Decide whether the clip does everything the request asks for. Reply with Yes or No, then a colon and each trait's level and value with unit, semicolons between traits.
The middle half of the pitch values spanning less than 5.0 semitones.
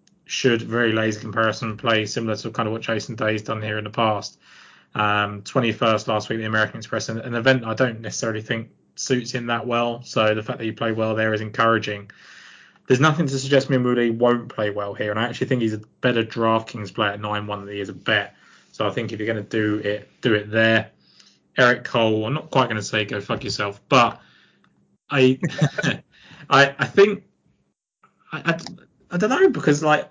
Yes: average, 2.8 semitones